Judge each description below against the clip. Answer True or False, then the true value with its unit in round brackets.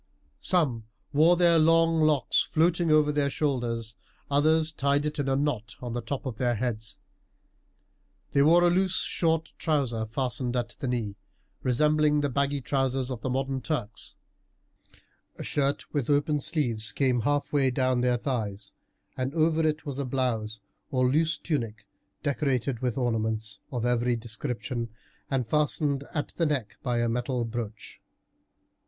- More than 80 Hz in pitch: True (135 Hz)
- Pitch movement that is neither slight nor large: True (4.0 semitones)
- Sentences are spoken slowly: False (150 wpm)